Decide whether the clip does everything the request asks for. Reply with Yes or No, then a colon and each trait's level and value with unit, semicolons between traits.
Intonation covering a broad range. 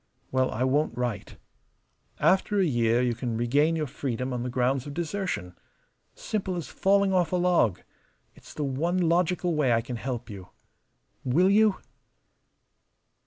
Yes: wide, 6.6 semitones